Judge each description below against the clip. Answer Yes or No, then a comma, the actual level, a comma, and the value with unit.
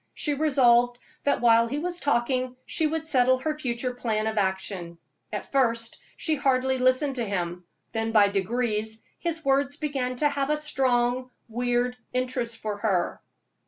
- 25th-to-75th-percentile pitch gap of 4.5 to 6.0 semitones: No, average, 3.4 semitones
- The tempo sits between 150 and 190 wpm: Yes, average, 160 wpm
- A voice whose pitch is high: Yes, very high, 250 Hz